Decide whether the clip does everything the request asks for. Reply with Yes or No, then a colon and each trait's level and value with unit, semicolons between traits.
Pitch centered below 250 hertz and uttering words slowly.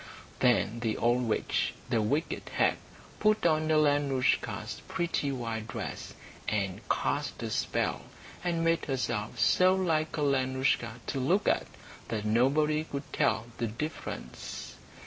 Yes: low, 135 Hz; slow, 125 wpm